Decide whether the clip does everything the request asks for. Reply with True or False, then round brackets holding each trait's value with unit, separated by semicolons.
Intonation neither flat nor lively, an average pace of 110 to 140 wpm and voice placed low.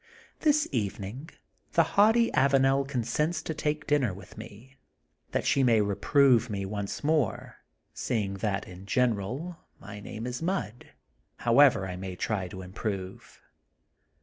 False (6.5 semitones; 135 wpm; 120 Hz)